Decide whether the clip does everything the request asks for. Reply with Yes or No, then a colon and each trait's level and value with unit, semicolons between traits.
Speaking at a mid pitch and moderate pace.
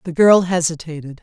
Yes: medium, 170 Hz; average, 145 wpm